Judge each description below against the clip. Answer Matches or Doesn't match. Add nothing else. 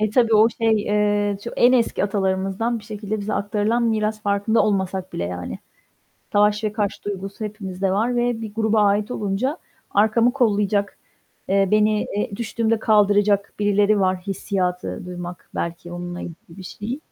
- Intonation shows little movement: Matches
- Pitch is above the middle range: Matches